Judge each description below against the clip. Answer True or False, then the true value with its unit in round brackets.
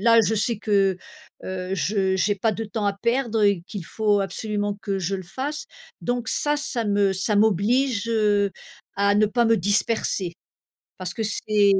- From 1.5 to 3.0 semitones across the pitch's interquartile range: True (2.4 semitones)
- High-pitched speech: True (205 Hz)